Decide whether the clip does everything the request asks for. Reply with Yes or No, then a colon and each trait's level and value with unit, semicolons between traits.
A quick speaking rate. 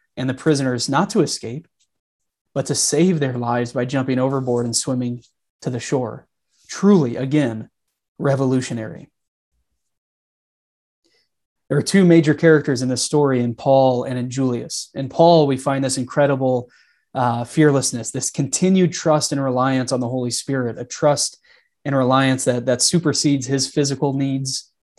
No: average, 150 wpm